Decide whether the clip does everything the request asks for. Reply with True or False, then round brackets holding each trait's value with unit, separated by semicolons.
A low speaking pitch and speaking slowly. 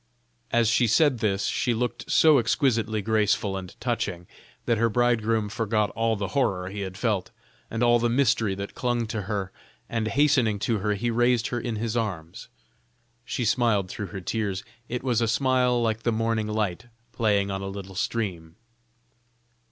False (110 Hz; 175 wpm)